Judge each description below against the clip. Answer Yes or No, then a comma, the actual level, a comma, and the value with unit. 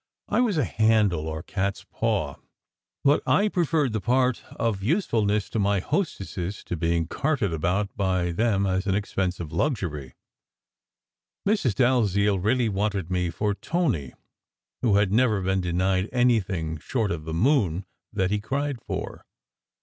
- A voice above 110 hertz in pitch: No, low, 100 Hz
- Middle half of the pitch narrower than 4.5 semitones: No, average, 5.0 semitones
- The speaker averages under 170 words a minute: Yes, average, 150 wpm